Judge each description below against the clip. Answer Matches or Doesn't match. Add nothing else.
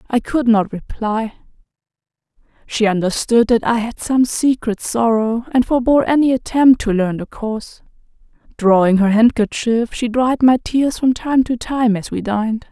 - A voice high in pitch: Matches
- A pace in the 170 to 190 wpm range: Doesn't match